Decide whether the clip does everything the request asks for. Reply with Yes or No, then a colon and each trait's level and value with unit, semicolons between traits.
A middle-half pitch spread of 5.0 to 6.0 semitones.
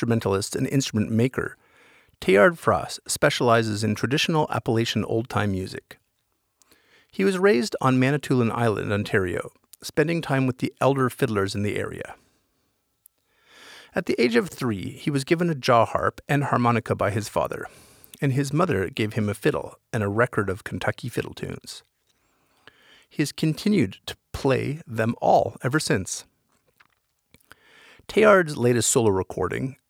Yes: wide, 5.4 semitones